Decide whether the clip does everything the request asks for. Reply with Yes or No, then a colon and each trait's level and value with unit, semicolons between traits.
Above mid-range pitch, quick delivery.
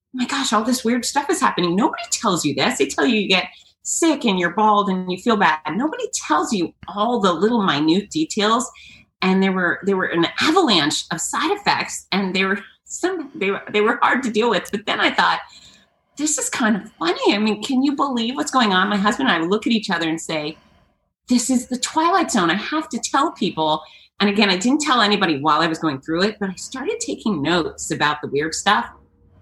Yes: high, 210 Hz; fast, 235 wpm